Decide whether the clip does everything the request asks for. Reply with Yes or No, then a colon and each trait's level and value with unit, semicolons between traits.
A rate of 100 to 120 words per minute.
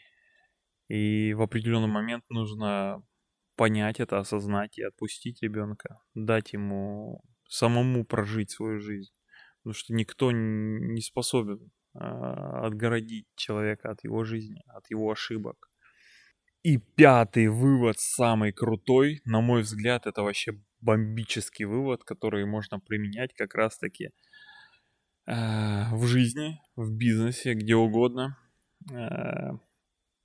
Yes: slow, 110 wpm